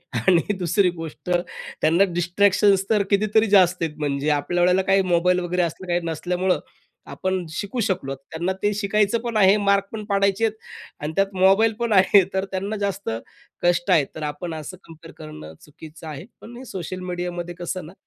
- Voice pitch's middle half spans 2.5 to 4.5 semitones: Yes, average, 3.0 semitones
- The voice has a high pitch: No, medium, 180 Hz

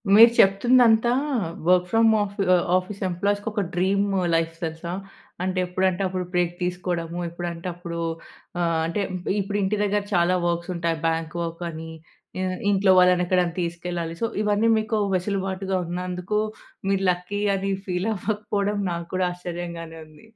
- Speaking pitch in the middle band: Yes, medium, 180 Hz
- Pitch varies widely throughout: No, average, 2.7 semitones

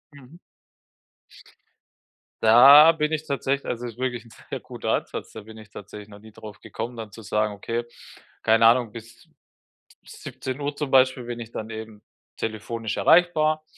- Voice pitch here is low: Yes, low, 115 Hz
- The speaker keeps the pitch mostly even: No, average, 3.9 semitones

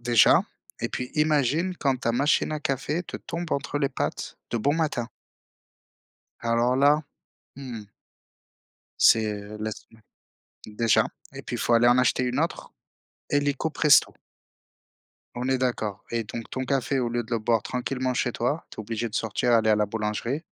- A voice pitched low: Yes, low, 125 Hz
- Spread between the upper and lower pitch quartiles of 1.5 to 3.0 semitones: No, average, 3.6 semitones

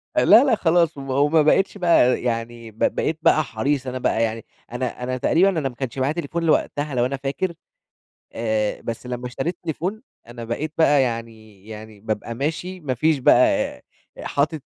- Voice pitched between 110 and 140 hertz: Yes, low, 135 Hz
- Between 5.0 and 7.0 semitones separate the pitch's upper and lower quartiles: Yes, average, 5.3 semitones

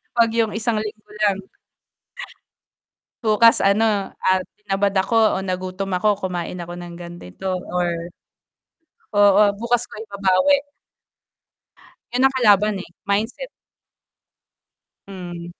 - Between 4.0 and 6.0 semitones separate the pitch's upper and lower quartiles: No, average, 3.0 semitones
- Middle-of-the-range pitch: No, high, 200 Hz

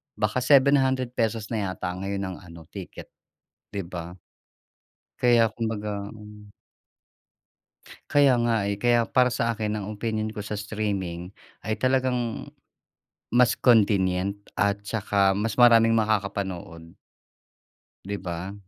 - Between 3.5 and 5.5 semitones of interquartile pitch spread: No, average, 3.0 semitones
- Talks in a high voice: No, low, 105 Hz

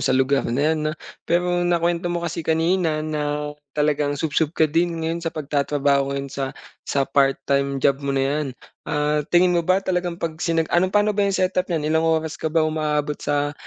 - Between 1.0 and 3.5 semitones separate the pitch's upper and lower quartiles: Yes, average, 3.1 semitones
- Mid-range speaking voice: Yes, medium, 155 Hz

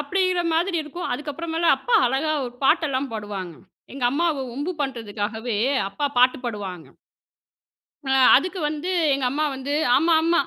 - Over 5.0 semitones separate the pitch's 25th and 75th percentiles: Yes, wide, 5.6 semitones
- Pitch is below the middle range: No, very high, 280 Hz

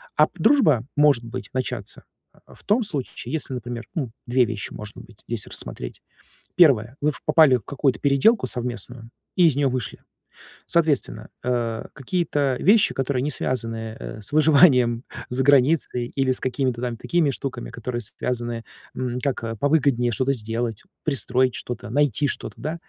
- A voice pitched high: No, low, 130 Hz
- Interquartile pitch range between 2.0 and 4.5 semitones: Yes, average, 3.3 semitones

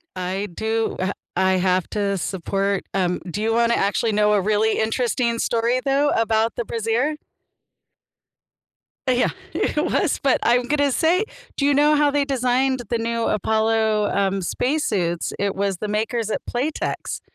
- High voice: Yes, high, 225 Hz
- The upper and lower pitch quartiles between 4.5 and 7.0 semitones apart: No, average, 4.0 semitones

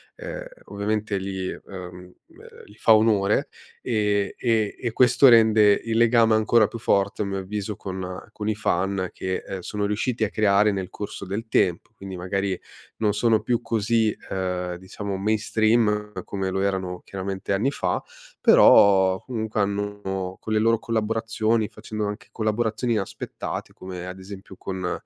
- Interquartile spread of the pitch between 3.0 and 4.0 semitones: No, narrow, 2.5 semitones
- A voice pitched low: Yes, low, 105 Hz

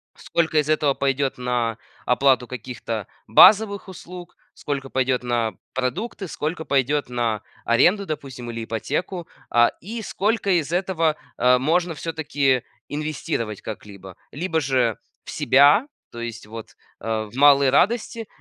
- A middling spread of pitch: No, wide, 5.7 semitones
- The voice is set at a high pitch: No, medium, 140 Hz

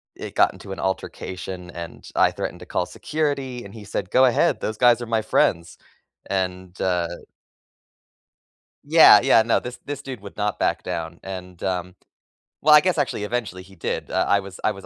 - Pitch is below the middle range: Yes, low, 100 Hz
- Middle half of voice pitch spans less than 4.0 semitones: No, average, 4.9 semitones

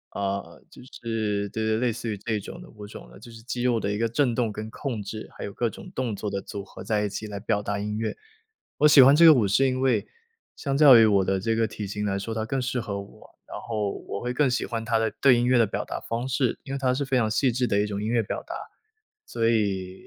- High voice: No, low, 115 Hz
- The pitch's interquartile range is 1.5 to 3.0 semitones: No, average, 3.4 semitones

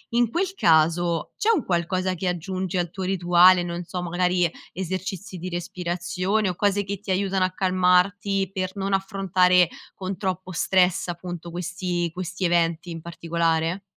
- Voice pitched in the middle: Yes, medium, 180 Hz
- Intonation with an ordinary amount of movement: No, narrow, 1.7 semitones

